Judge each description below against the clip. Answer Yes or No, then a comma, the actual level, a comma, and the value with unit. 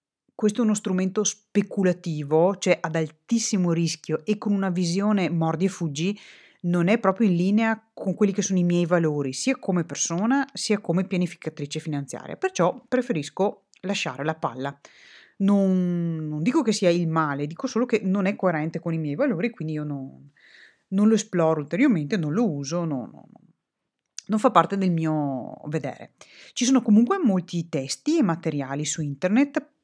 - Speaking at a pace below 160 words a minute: No, fast, 170 wpm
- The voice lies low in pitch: No, medium, 180 Hz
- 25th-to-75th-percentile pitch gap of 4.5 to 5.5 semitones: Yes, average, 4.9 semitones